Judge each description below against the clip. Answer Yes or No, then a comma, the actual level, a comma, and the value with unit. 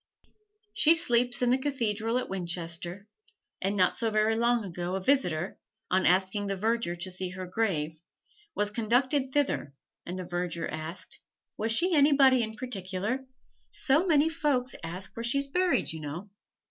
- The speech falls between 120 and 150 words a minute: No, average, 160 wpm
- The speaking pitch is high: Yes, high, 215 Hz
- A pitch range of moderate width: No, wide, 6.1 semitones